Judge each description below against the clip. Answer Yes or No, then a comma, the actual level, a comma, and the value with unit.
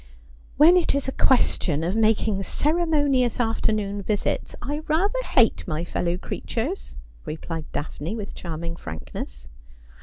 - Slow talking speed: Yes, slow, 130 wpm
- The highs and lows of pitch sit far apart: Yes, wide, 8.7 semitones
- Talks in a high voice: Yes, high, 220 Hz